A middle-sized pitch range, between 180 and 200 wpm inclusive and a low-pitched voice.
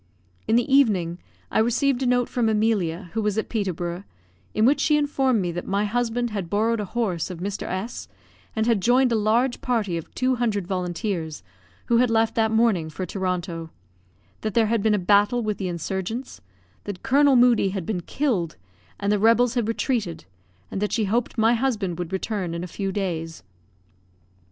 No: average, 4.4 semitones; average, 190 wpm; high, 215 Hz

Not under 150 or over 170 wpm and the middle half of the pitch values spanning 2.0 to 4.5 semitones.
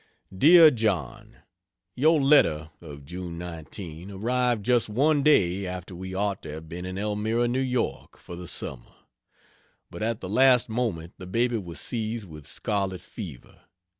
No: average, 155 wpm; wide, 5.6 semitones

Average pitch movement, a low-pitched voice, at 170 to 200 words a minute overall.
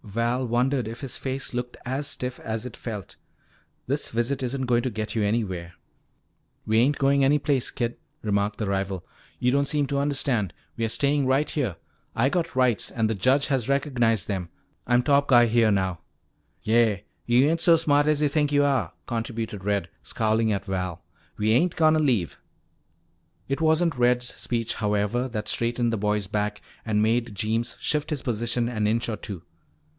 Yes: average, 4.2 semitones; low, 120 Hz; average, 180 wpm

